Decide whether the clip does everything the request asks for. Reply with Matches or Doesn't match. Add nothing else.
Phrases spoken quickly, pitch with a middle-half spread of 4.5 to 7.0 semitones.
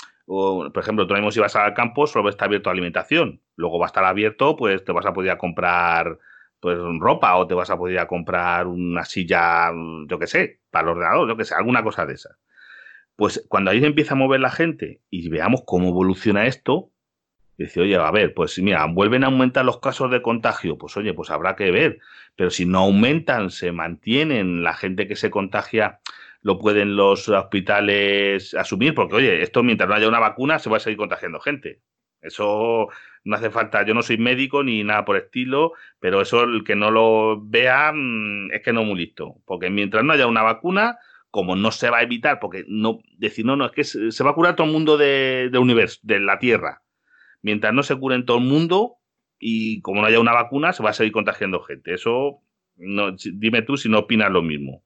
Matches